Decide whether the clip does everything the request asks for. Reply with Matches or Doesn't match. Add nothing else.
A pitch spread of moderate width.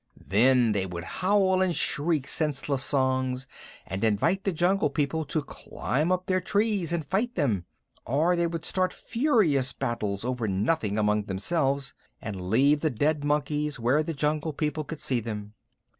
Doesn't match